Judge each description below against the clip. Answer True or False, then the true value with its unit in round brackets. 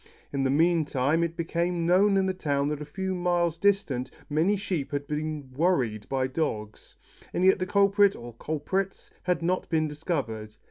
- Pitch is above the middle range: False (160 Hz)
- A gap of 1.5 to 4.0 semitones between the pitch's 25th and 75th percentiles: False (4.6 semitones)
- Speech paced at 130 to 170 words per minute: False (185 wpm)